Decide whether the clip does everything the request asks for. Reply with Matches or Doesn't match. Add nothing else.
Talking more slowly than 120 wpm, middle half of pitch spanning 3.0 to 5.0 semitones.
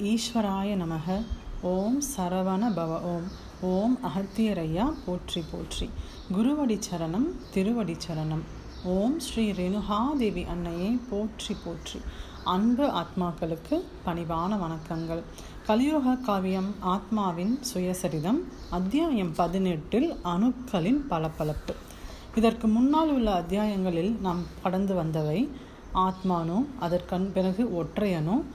Matches